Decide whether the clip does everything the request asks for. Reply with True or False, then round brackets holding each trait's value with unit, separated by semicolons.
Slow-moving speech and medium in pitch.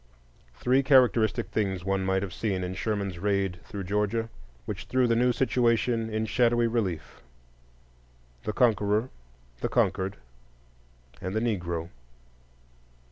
False (125 wpm; 105 Hz)